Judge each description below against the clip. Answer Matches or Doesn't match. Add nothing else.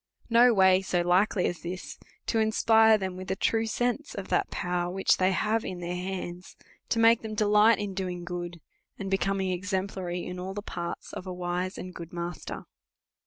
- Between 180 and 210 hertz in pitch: Matches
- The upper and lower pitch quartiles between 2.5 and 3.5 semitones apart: Matches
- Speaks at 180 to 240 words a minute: Matches